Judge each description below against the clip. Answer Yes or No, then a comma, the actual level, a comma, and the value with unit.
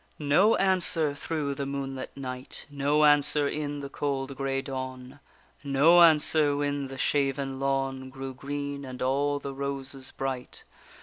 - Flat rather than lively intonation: Yes, narrow, 1.3 semitones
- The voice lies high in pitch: No, medium, 140 Hz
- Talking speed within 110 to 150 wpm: Yes, average, 140 wpm